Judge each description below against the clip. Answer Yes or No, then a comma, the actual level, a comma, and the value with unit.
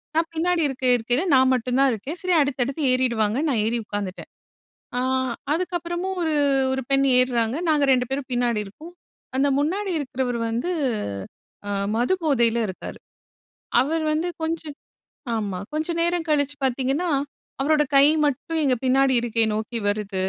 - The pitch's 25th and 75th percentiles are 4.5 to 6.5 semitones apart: Yes, average, 4.9 semitones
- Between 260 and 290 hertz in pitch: Yes, very high, 270 Hz